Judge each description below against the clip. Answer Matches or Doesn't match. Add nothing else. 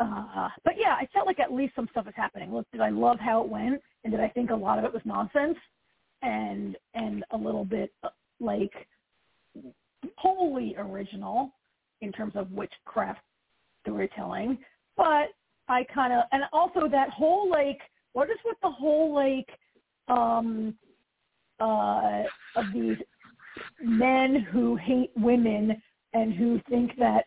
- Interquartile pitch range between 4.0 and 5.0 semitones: Matches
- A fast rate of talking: Doesn't match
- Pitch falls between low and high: Doesn't match